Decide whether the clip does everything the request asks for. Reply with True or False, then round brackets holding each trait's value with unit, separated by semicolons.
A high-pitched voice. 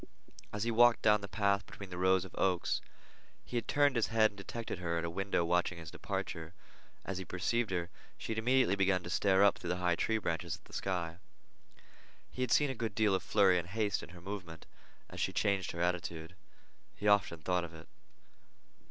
False (95 Hz)